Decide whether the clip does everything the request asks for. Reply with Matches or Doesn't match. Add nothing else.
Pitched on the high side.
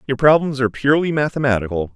Doesn't match